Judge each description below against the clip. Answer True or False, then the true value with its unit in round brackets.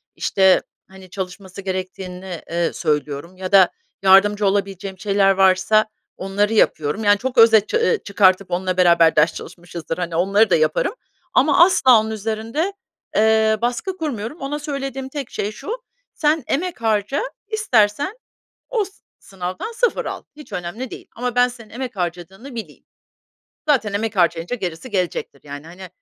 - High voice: True (205 Hz)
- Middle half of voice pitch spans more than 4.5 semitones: True (5.2 semitones)